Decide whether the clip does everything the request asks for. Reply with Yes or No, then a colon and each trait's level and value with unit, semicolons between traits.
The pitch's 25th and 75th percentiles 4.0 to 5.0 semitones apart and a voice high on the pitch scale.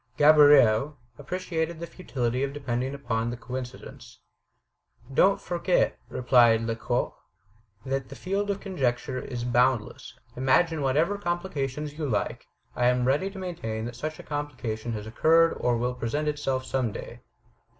No: average, 4.4 semitones; low, 135 Hz